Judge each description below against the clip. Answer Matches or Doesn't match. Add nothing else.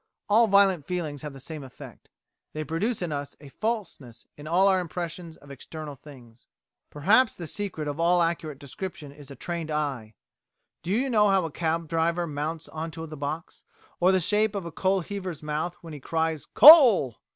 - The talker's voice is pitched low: Doesn't match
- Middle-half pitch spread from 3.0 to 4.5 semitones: Matches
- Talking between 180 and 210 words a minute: Matches